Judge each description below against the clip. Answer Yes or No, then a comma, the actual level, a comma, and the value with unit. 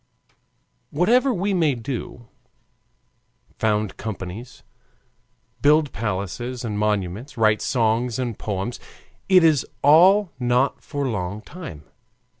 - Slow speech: Yes, slow, 100 wpm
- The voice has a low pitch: Yes, low, 120 Hz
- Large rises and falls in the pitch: Yes, wide, 5.9 semitones